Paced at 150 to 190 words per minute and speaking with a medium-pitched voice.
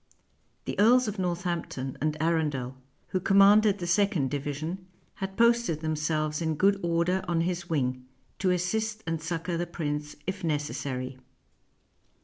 No: slow, 135 wpm; medium, 170 Hz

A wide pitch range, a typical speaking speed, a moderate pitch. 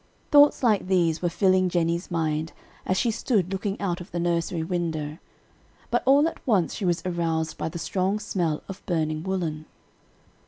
No: average, 2.9 semitones; average, 170 wpm; medium, 175 Hz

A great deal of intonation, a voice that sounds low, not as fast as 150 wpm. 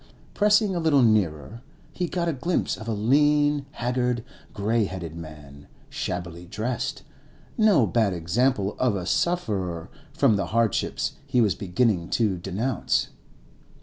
Yes: wide, 6.7 semitones; low, 110 Hz; slow, 135 wpm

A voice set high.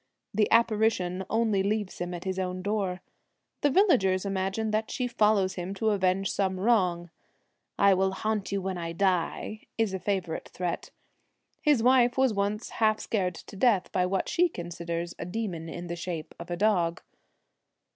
Yes: high, 195 Hz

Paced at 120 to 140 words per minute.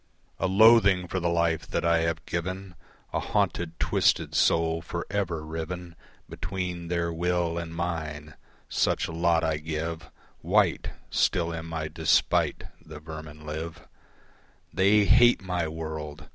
Yes: slow, 135 wpm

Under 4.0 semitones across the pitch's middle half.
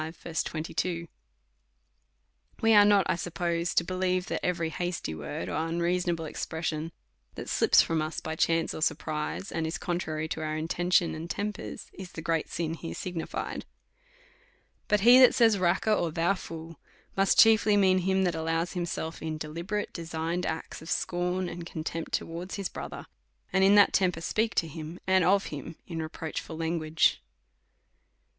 Yes: narrow, 2.4 semitones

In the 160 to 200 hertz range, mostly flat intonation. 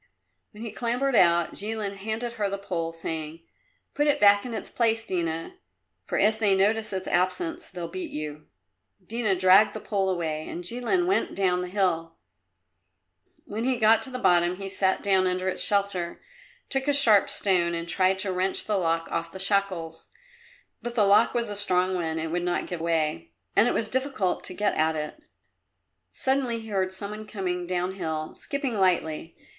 No: high, 190 Hz; average, 4.1 semitones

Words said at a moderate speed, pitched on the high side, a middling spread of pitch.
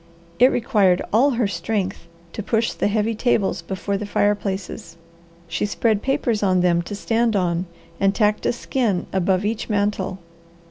Yes: average, 155 wpm; high, 205 Hz; average, 3.0 semitones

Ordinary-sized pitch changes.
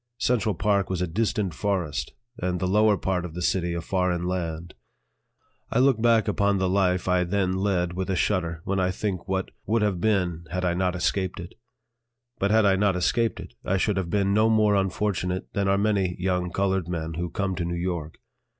No: narrow, 2.3 semitones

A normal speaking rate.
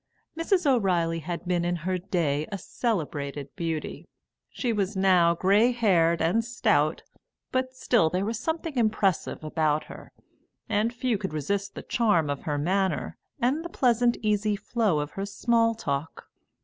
Yes: average, 155 wpm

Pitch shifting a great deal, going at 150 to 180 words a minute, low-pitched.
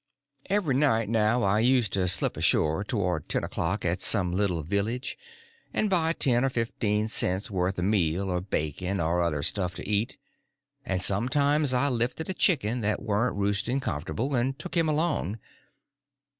Yes: wide, 5.8 semitones; average, 165 wpm; low, 105 Hz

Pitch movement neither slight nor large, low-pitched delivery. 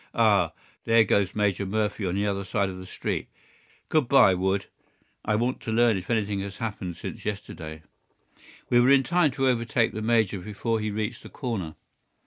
Yes: average, 3.1 semitones; low, 105 Hz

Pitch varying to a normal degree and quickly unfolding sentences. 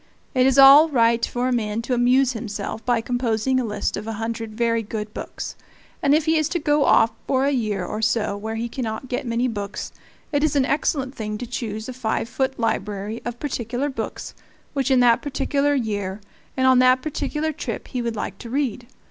Yes: average, 3.3 semitones; fast, 210 wpm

